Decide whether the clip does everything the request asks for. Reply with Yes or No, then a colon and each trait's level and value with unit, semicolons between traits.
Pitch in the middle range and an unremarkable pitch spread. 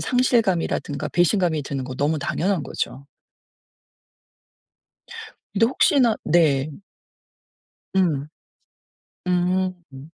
Yes: medium, 170 Hz; average, 4.8 semitones